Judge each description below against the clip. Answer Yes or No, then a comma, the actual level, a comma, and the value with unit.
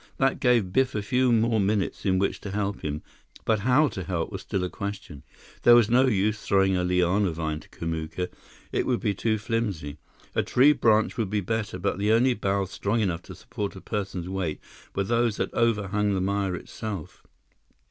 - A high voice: No, low, 100 Hz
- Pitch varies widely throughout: No, average, 3.4 semitones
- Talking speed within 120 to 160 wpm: No, average, 200 wpm